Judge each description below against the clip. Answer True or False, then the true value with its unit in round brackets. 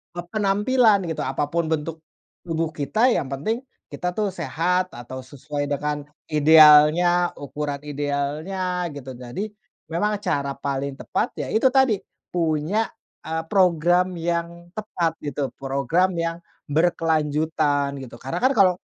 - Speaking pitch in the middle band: True (160 Hz)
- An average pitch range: True (4.0 semitones)